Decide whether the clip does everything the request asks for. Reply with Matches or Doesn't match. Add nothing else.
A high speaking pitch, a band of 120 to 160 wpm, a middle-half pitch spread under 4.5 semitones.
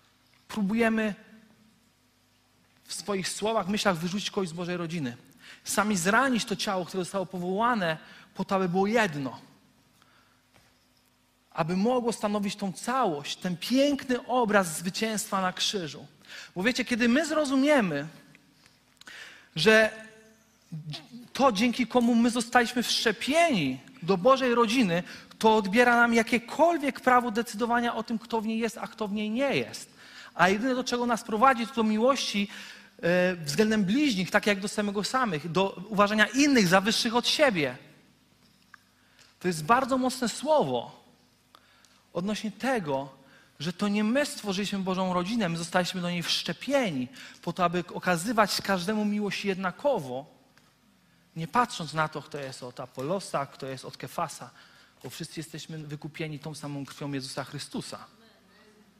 Doesn't match